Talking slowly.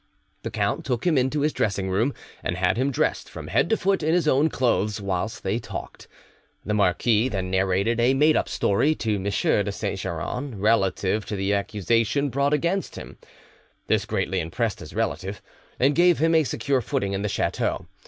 No: average, 190 wpm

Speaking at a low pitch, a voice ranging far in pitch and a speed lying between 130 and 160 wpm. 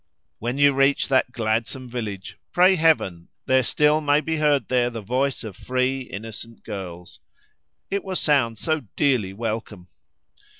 No: low, 125 Hz; average, 4.6 semitones; average, 145 wpm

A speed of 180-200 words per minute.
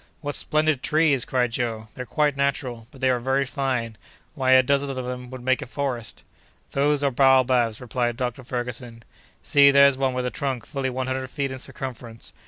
Yes: average, 190 wpm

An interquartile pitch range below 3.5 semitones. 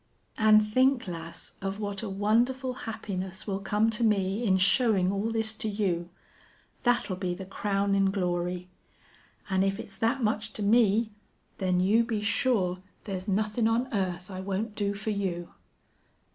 Yes: average, 2.8 semitones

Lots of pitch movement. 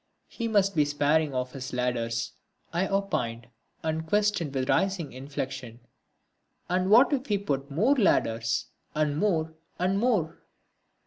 Yes: wide, 7.1 semitones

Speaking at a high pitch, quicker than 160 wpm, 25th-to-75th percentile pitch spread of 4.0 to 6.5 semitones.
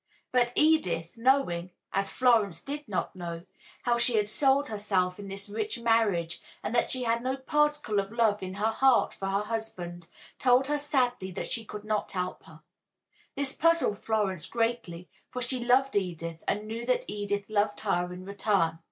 Yes: high, 215 Hz; average, 180 wpm; average, 4.5 semitones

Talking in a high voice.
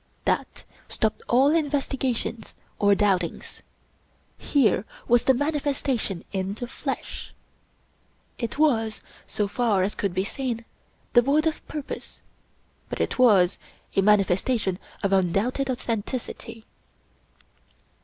Yes: high, 230 Hz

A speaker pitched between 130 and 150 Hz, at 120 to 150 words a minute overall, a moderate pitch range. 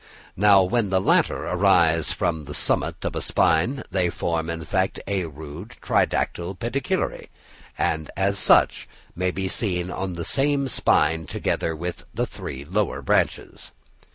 No: very low, 90 Hz; average, 145 wpm; average, 3.5 semitones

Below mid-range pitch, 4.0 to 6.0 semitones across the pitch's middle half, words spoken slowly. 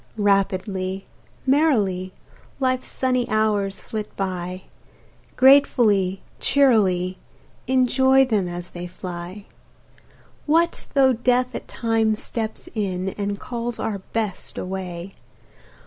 No: high, 210 Hz; average, 5.1 semitones; slow, 100 wpm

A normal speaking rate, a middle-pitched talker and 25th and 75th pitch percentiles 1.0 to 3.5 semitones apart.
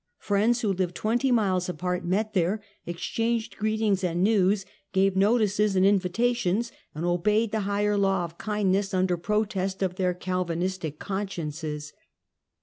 No: average, 145 wpm; high, 195 Hz; average, 2.8 semitones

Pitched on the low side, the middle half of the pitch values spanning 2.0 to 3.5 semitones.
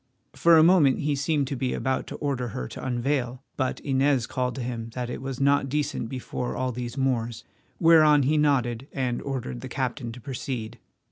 Yes: low, 130 Hz; average, 2.7 semitones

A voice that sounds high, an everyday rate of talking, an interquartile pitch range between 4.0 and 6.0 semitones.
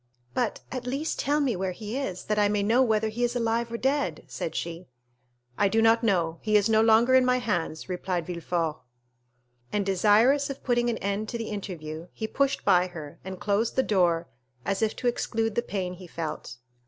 No: high, 210 Hz; fast, 210 wpm; average, 4.8 semitones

